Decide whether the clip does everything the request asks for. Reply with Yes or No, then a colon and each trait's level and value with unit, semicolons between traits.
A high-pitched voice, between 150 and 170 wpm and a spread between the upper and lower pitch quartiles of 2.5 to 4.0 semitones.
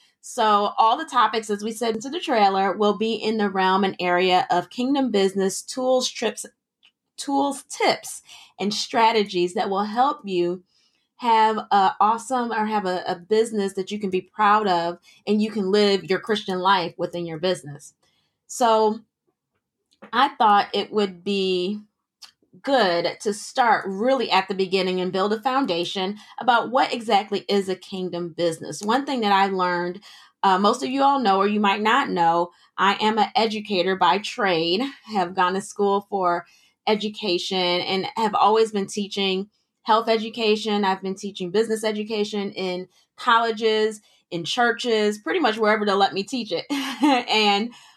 Yes: high, 205 Hz; average, 165 wpm; average, 3.0 semitones